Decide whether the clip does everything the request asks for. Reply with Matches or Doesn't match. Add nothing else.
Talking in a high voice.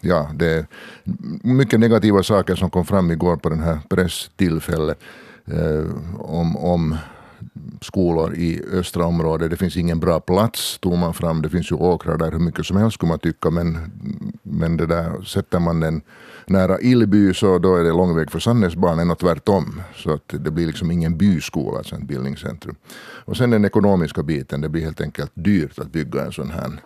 Doesn't match